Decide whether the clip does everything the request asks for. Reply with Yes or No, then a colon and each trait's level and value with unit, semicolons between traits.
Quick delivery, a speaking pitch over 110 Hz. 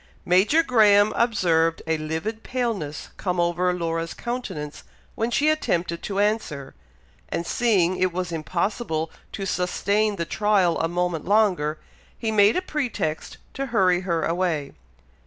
No: average, 140 wpm; medium, 185 Hz